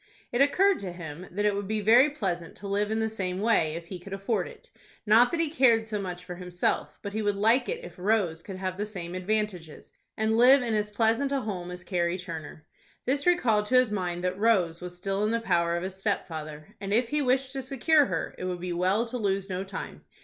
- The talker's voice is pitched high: Yes, high, 200 Hz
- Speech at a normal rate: No, fast, 240 wpm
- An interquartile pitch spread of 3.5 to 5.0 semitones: Yes, average, 4.3 semitones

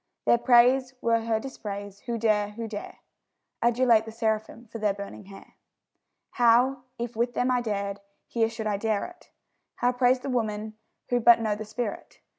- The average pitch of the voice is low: No, high, 230 Hz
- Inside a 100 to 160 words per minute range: No, average, 175 wpm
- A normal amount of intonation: No, narrow, 2.3 semitones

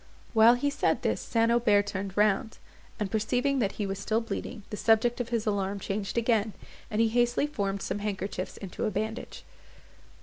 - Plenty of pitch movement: No, average, 2.7 semitones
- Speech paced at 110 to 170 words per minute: No, average, 180 wpm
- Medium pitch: No, high, 215 Hz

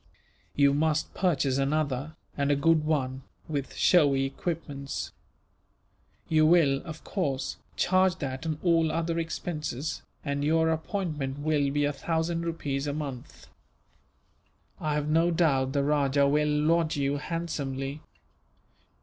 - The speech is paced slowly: Yes, slow, 130 wpm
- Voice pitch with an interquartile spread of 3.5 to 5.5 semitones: No, average, 2.7 semitones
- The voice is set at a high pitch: No, medium, 150 Hz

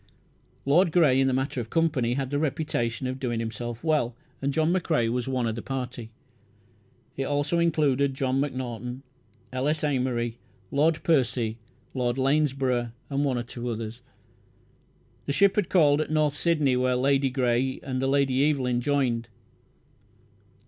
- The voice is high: No, low, 135 Hz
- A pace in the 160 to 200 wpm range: No, average, 150 wpm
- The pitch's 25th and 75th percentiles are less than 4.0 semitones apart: Yes, average, 3.0 semitones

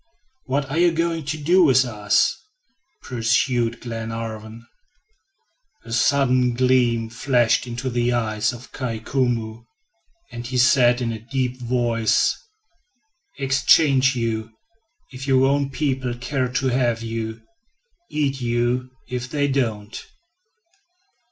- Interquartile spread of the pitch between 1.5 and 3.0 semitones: Yes, narrow, 2.6 semitones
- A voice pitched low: Yes, low, 125 Hz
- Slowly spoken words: Yes, slow, 120 wpm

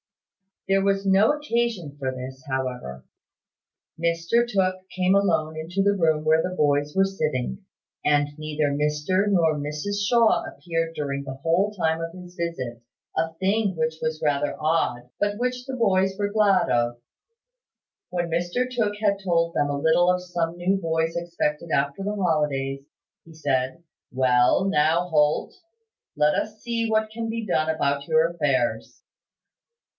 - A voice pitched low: No, medium, 165 Hz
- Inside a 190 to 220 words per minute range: No, average, 155 wpm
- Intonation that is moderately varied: Yes, average, 4.8 semitones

